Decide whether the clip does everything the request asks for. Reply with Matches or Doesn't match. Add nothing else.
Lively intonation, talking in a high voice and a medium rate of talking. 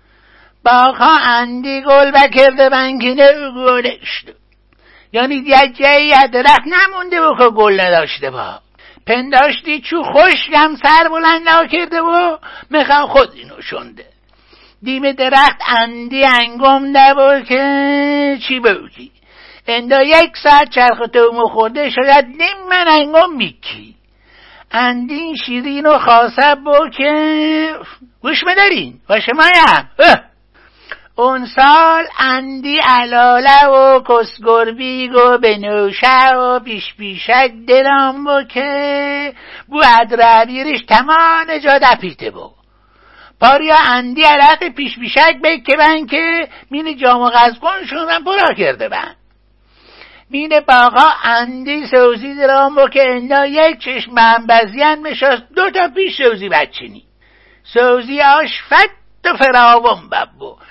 Doesn't match